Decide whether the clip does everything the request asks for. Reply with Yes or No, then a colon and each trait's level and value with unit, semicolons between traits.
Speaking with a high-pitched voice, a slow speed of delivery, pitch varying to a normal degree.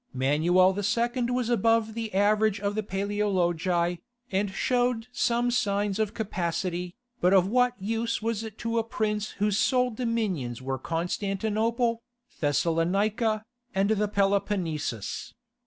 Yes: high, 205 Hz; slow, 125 wpm; average, 3.7 semitones